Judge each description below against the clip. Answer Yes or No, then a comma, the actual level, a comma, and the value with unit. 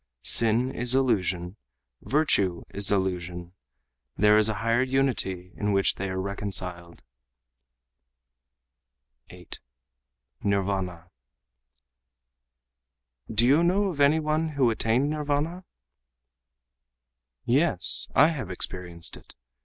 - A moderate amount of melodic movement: No, wide, 7.1 semitones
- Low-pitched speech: Yes, low, 110 Hz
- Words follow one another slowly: Yes, slow, 100 wpm